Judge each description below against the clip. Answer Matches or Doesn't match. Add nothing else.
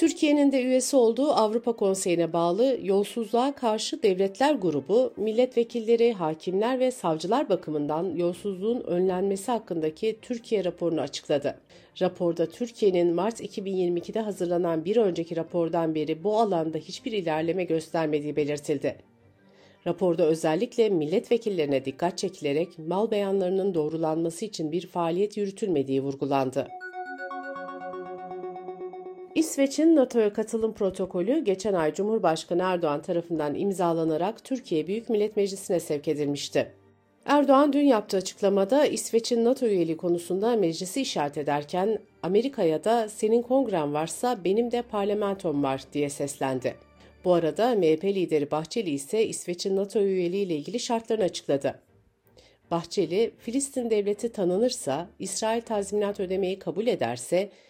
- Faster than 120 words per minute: Doesn't match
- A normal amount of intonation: Doesn't match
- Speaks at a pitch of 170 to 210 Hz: Matches